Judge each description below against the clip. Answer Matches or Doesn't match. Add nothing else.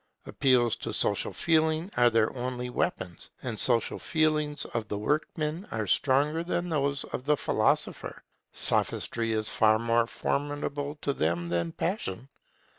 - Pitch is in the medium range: Doesn't match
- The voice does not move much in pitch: Doesn't match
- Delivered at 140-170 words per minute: Matches